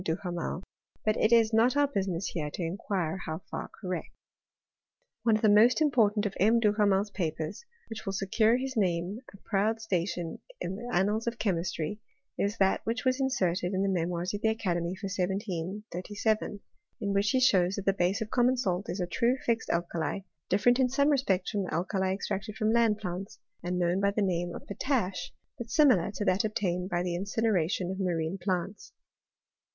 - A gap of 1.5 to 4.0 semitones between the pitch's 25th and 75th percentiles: Yes, average, 3.6 semitones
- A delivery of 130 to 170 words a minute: No, average, 190 wpm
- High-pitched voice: Yes, high, 195 Hz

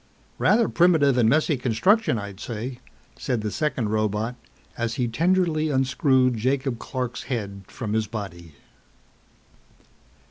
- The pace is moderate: No, slow, 120 wpm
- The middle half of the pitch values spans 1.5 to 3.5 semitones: No, average, 4.6 semitones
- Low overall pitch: Yes, low, 125 Hz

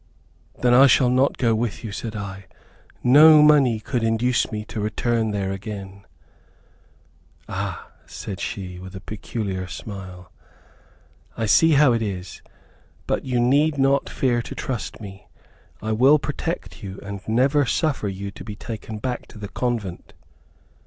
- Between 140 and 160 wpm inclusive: Yes, average, 150 wpm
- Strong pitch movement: No, average, 4.4 semitones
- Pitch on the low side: Yes, low, 110 Hz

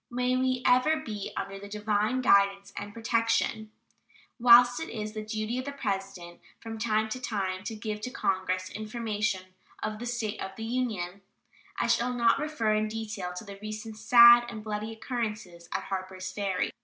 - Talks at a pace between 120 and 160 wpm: No, average, 175 wpm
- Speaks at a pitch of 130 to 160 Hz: No, high, 215 Hz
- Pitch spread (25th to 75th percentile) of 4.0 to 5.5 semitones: No, average, 3.1 semitones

